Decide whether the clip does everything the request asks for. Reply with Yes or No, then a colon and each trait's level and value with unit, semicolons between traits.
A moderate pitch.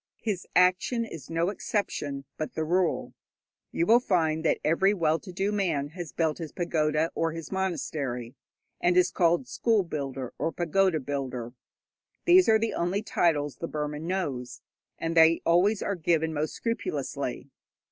Yes: medium, 165 Hz